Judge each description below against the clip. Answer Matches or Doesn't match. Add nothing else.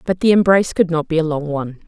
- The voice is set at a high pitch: Doesn't match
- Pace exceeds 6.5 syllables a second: Matches